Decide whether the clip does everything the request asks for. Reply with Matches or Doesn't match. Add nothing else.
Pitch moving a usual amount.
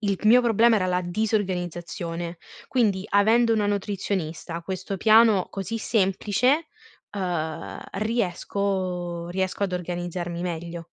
Matches